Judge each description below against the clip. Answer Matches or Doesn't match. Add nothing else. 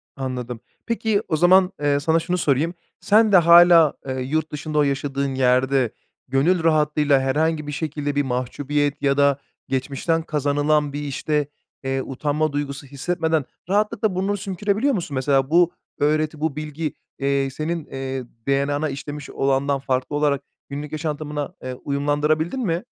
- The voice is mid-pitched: Matches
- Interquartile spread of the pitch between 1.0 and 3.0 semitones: Matches